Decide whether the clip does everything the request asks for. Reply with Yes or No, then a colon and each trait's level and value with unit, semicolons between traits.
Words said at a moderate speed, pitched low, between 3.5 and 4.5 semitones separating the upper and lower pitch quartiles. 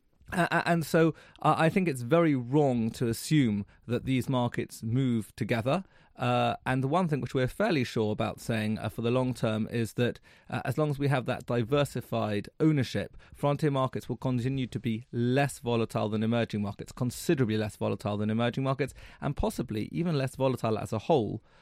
Yes: average, 190 wpm; low, 125 Hz; average, 3.9 semitones